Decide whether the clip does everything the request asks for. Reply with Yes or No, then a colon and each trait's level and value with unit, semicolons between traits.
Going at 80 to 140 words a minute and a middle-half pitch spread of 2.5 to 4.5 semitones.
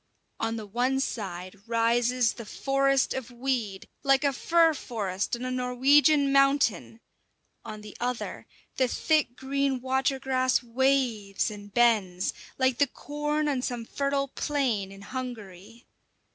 Yes: slow, 135 wpm; average, 3.4 semitones